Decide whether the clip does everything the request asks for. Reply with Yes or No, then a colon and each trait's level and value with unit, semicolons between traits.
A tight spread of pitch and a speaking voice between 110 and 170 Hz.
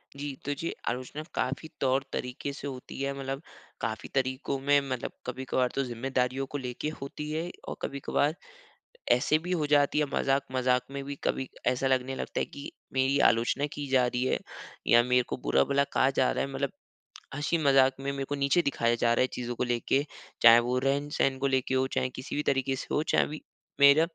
Yes: narrow, 1.8 semitones; low, 135 Hz